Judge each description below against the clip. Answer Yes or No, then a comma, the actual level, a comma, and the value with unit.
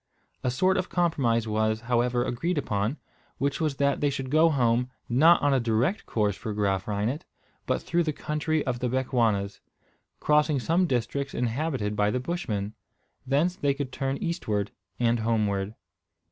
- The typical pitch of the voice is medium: No, low, 125 Hz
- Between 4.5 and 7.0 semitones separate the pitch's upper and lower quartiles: Yes, average, 5.2 semitones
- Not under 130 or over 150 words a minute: No, average, 160 wpm